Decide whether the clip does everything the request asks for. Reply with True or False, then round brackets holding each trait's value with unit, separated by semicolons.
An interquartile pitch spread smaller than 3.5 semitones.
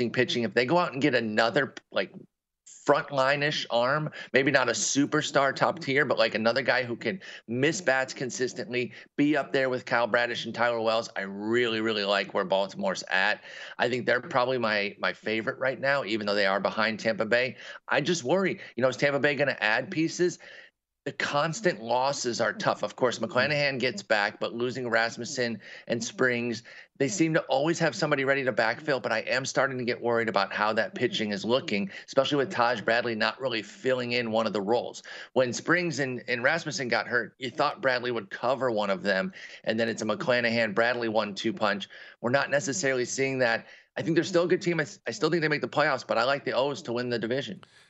False (3.8 semitones)